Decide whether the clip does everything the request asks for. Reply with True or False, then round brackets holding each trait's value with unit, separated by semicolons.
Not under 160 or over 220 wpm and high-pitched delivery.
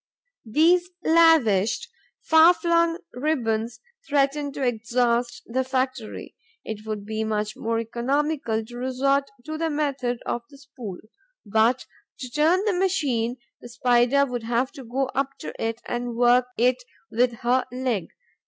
False (145 wpm; 250 Hz)